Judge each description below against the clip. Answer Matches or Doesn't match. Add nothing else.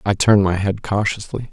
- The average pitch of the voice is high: Doesn't match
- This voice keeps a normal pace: Matches